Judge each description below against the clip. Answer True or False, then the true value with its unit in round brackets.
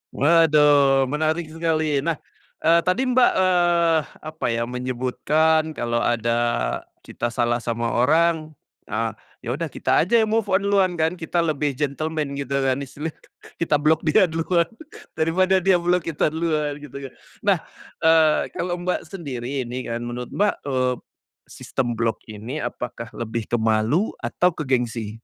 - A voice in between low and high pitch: True (150 Hz)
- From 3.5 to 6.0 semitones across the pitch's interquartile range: True (5.3 semitones)